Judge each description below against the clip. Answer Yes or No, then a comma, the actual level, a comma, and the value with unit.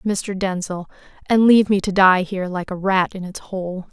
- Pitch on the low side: No, high, 190 Hz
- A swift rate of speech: Yes, fast, 215 wpm